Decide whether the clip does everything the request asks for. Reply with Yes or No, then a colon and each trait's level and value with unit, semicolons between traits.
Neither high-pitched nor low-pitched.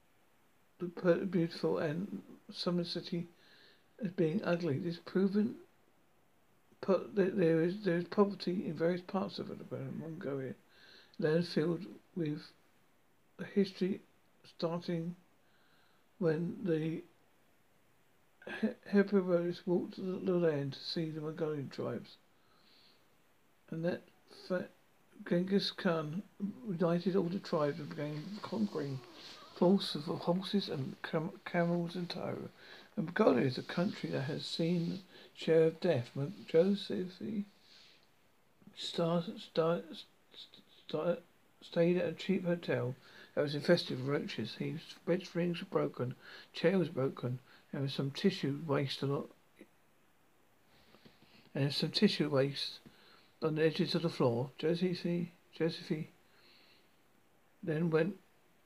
Yes: medium, 175 Hz